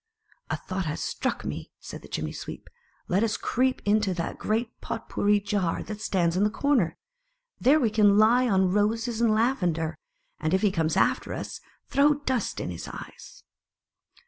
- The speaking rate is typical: Yes, average, 185 wpm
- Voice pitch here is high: Yes, high, 210 Hz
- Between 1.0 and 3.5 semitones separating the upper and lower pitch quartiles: No, average, 3.9 semitones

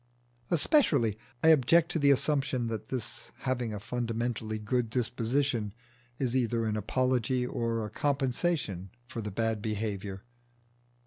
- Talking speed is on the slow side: Yes, slow, 130 wpm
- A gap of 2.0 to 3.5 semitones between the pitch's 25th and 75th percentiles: Yes, average, 3.2 semitones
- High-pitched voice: No, low, 120 Hz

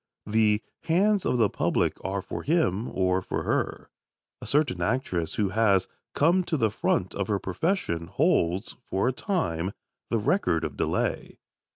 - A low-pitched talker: Yes, low, 105 Hz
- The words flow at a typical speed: Yes, average, 160 wpm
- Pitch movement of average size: No, wide, 8.5 semitones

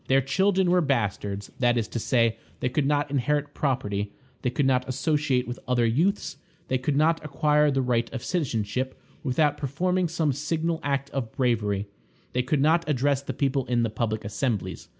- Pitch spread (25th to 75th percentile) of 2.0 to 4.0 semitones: Yes, average, 3.7 semitones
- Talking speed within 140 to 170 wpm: No, average, 180 wpm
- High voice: No, low, 135 Hz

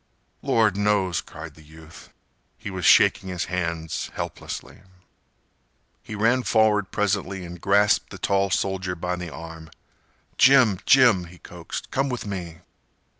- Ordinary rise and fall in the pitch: Yes, average, 3.4 semitones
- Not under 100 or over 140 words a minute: Yes, slow, 135 wpm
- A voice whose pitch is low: Yes, very low, 95 Hz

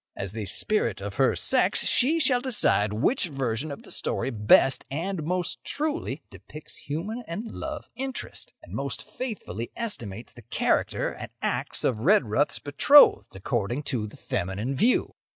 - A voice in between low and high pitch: Yes, medium, 145 Hz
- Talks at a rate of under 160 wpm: Yes, average, 150 wpm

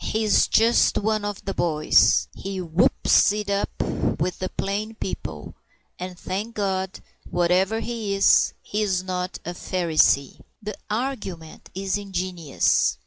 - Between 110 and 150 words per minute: Yes, average, 140 wpm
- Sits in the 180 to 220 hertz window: Yes, high, 190 Hz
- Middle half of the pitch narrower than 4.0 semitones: Yes, average, 2.8 semitones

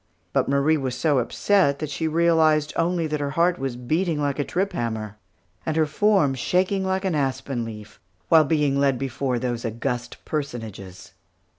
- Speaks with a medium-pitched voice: Yes, medium, 145 Hz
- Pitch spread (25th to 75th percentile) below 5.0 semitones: Yes, average, 4.5 semitones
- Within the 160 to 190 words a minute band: Yes, average, 170 wpm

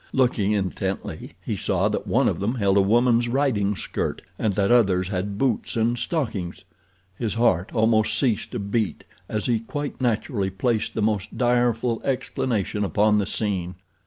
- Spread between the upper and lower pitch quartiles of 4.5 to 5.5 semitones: No, average, 3.3 semitones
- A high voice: No, low, 110 Hz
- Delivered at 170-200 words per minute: No, average, 160 wpm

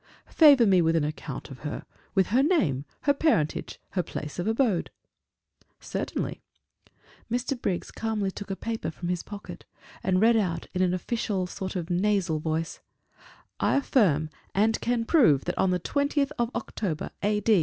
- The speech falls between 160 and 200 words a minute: Yes, average, 165 wpm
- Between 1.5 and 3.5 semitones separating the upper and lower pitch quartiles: No, wide, 5.6 semitones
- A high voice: Yes, high, 195 Hz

